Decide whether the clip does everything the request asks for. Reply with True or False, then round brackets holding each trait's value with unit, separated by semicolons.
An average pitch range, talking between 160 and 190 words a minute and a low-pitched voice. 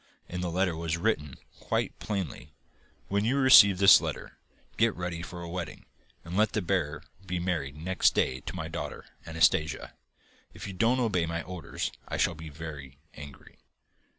True (3.3 semitones; 170 wpm; 85 Hz)